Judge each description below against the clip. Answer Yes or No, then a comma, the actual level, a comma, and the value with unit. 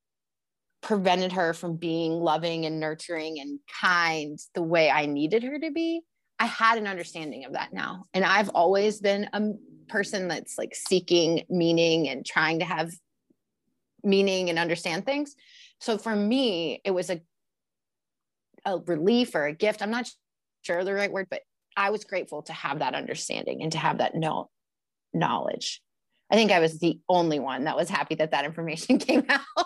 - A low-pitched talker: No, medium, 185 Hz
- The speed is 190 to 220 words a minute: No, average, 175 wpm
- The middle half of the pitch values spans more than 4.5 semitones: Yes, average, 4.9 semitones